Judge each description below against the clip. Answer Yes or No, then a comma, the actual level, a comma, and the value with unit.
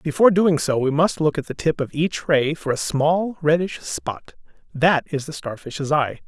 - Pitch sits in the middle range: Yes, medium, 150 Hz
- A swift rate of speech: Yes, fast, 210 wpm